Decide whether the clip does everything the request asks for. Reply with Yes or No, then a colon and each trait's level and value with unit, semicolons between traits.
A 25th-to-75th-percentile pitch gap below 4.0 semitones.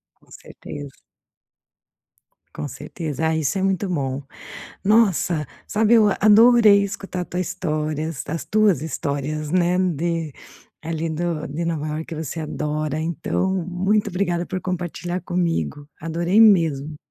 Yes: average, 3.5 semitones